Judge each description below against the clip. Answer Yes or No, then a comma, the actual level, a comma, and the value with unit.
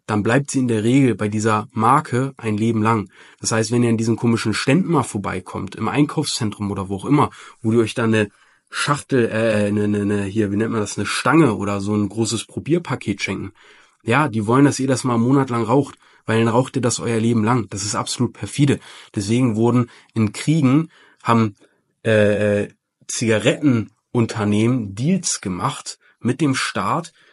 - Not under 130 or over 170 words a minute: No, fast, 190 wpm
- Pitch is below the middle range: Yes, low, 115 Hz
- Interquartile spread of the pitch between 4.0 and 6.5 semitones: No, average, 3.3 semitones